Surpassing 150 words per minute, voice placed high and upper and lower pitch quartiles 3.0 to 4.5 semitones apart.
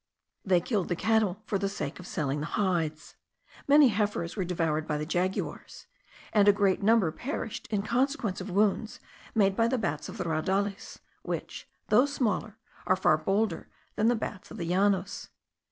Yes: average, 175 wpm; high, 195 Hz; average, 3.8 semitones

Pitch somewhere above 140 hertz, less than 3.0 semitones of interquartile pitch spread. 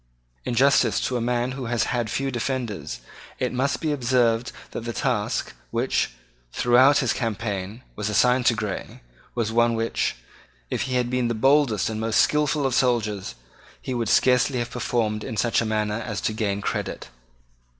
No: low, 120 Hz; narrow, 2.6 semitones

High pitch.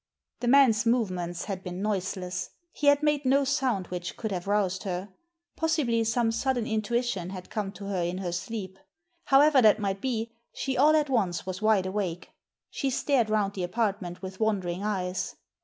Yes: high, 210 Hz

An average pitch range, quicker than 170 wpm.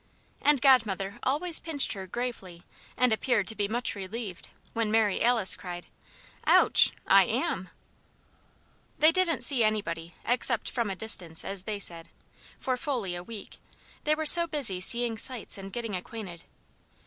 No: average, 4.7 semitones; average, 150 wpm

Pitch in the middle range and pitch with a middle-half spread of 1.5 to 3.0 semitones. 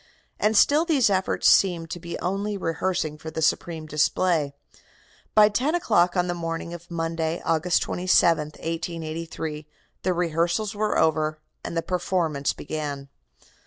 Yes: medium, 170 Hz; average, 2.7 semitones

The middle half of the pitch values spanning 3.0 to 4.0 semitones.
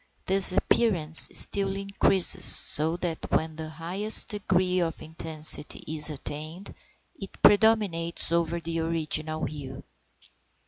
Yes: average, 3.5 semitones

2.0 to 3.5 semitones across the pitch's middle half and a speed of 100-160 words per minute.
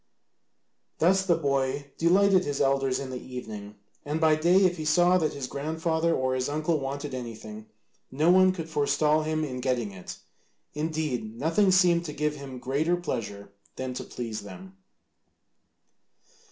No: average, 4.4 semitones; average, 155 wpm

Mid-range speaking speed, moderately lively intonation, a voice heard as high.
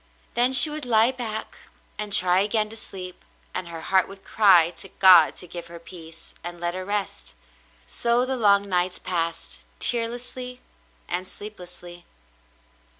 Yes: average, 150 wpm; average, 4.4 semitones; high, 195 Hz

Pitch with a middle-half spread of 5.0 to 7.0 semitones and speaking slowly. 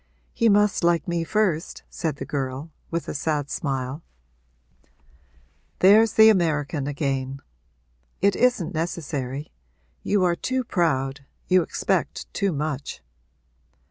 Yes: average, 5.3 semitones; slow, 115 wpm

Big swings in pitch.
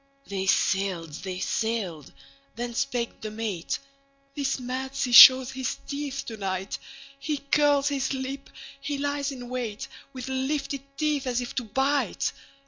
No: average, 3.6 semitones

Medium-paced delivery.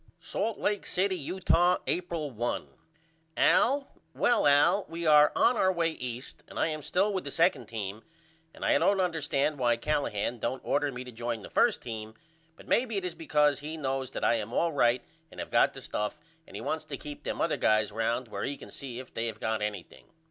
No: fast, 215 wpm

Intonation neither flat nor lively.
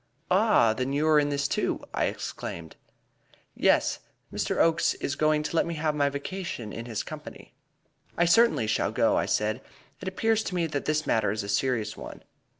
No: wide, 6.5 semitones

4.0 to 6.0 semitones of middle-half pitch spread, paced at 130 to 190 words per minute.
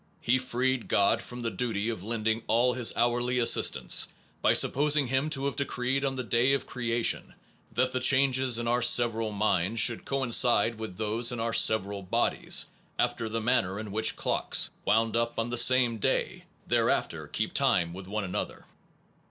No: narrow, 2.4 semitones; average, 180 wpm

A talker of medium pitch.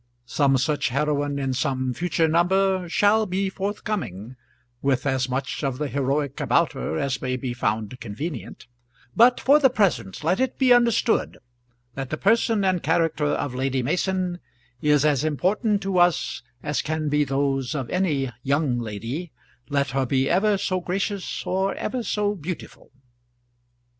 Yes: medium, 150 Hz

